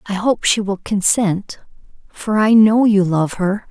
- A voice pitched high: Yes, high, 205 Hz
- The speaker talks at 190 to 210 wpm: No, average, 180 wpm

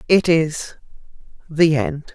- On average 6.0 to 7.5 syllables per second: No, 3.2 syllables/s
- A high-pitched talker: No, medium, 155 Hz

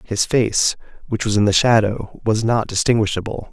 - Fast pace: No, average, 170 wpm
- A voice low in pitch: Yes, low, 110 Hz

